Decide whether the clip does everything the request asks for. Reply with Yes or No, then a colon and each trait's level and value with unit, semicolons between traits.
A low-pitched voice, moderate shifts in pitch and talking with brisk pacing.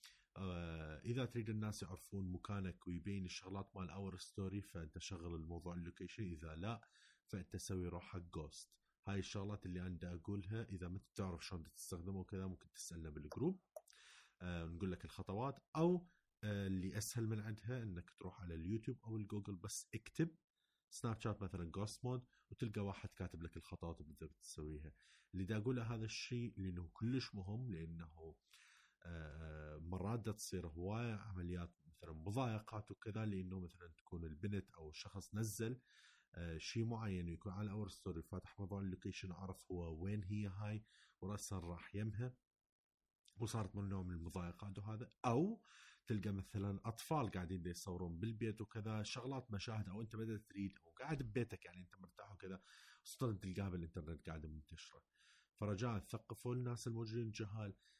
Yes: low, 100 Hz; average, 3.7 semitones; fast, 145 wpm